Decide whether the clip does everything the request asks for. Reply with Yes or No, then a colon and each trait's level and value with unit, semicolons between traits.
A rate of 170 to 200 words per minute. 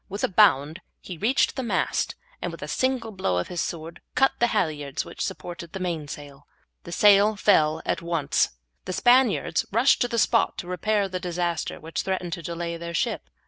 Yes: average, 195 wpm